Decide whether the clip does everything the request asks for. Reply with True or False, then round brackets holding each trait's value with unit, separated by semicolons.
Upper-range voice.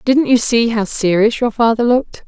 True (230 Hz)